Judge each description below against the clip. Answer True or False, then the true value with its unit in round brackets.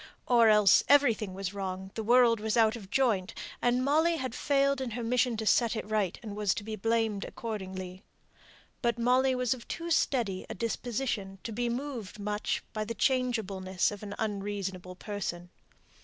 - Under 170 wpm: False (175 wpm)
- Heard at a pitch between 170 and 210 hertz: False (220 Hz)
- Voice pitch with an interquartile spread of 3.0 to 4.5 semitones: True (3.7 semitones)